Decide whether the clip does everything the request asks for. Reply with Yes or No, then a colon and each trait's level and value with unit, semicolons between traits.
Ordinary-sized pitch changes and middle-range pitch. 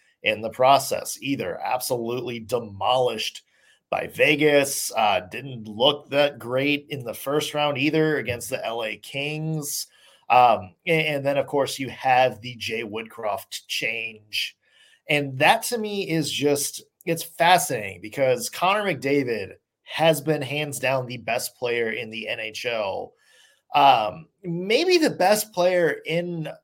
Yes: average, 4.2 semitones; medium, 145 Hz